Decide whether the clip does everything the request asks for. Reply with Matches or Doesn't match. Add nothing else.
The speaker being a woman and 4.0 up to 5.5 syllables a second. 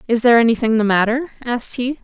Doesn't match